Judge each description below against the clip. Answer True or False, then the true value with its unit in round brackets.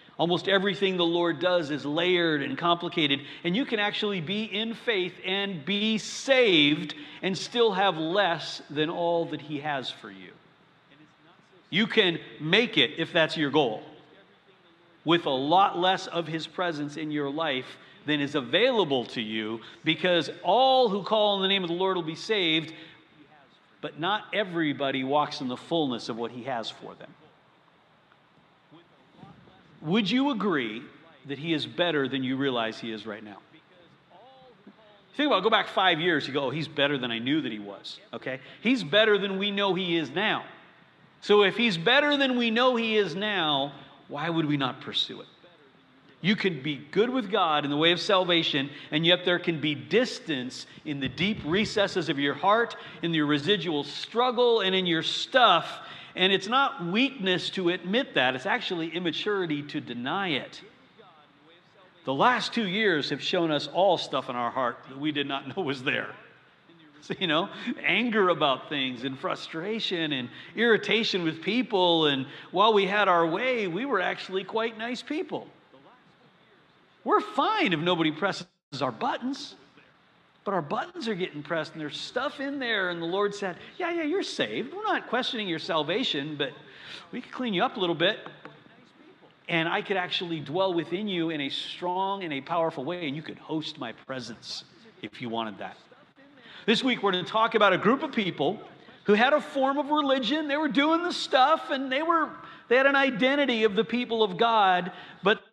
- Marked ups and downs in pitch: True (5.9 semitones)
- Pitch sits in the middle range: True (180 Hz)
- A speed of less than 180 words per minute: False (185 wpm)